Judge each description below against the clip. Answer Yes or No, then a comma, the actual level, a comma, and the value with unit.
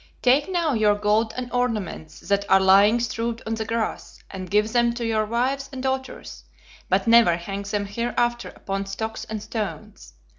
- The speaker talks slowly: No, average, 175 wpm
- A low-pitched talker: No, high, 220 Hz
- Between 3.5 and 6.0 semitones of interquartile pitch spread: No, average, 2.8 semitones